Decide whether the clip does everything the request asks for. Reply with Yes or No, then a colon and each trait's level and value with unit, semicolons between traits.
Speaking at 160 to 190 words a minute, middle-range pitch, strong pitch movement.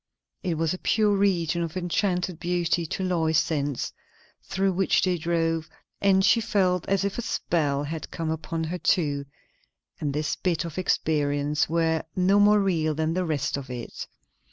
No: average, 170 wpm; medium, 170 Hz; average, 3.0 semitones